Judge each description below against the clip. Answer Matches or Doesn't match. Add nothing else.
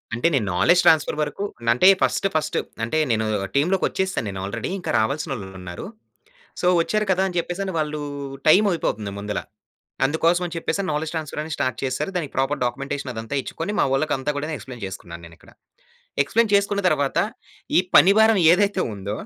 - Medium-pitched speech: Matches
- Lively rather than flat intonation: Matches